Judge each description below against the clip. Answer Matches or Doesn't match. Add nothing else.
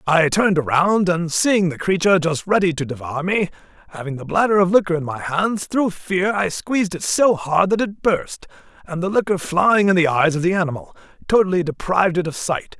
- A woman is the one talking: Doesn't match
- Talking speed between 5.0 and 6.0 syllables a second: Matches